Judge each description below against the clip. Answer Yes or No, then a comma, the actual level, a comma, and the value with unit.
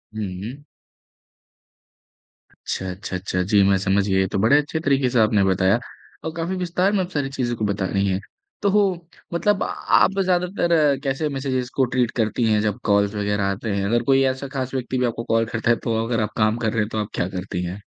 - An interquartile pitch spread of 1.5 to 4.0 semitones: No, wide, 5.6 semitones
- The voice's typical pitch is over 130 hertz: No, low, 115 Hz